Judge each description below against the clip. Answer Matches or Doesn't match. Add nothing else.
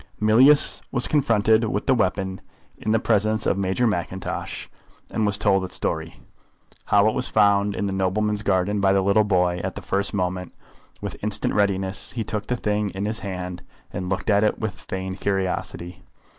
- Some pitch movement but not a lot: Doesn't match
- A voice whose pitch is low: Matches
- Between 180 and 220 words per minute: Matches